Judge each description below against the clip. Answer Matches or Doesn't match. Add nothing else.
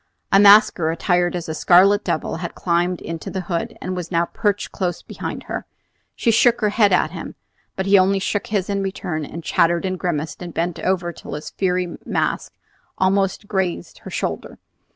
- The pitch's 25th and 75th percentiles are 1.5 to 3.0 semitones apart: Matches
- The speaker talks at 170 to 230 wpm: Matches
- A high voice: Doesn't match